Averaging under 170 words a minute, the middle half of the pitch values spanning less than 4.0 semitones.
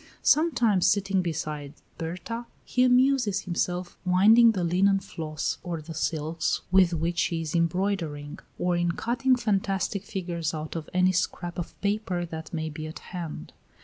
Yes: average, 150 wpm; average, 3.5 semitones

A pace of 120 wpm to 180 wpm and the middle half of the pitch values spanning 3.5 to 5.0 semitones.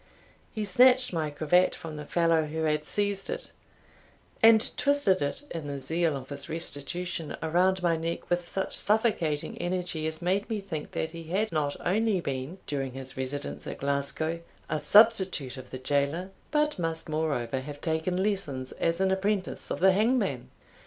Yes: average, 170 wpm; average, 4.7 semitones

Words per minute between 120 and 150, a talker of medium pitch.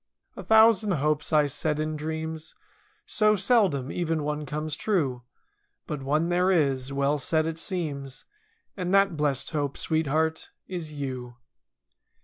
Yes: slow, 135 wpm; medium, 155 Hz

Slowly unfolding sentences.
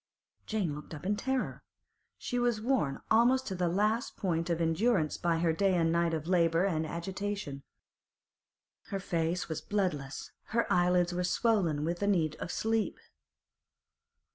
No: average, 155 wpm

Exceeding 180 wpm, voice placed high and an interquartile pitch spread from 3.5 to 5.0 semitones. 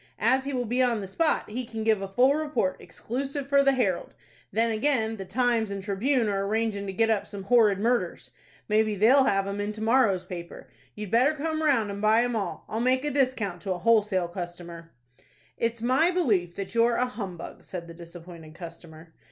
Yes: fast, 205 wpm; high, 220 Hz; average, 4.5 semitones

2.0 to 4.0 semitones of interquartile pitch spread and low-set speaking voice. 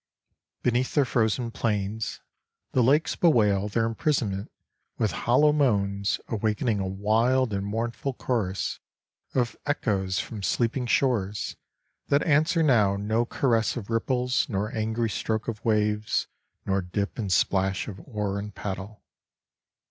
Yes: average, 3.5 semitones; low, 110 Hz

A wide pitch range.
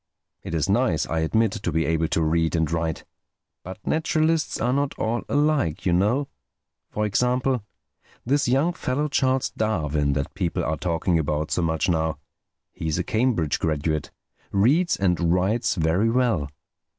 Yes: wide, 7.6 semitones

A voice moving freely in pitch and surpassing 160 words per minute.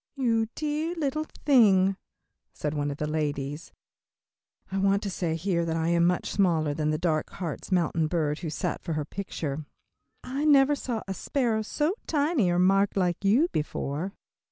Yes: wide, 7.0 semitones; average, 175 wpm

